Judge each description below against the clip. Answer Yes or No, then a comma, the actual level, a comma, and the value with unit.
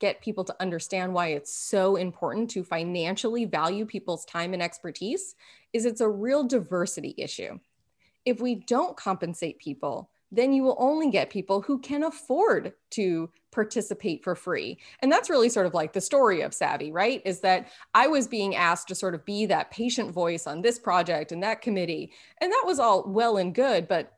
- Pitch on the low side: No, high, 195 Hz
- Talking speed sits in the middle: Yes, average, 190 wpm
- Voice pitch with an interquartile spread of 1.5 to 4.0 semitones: No, average, 5.0 semitones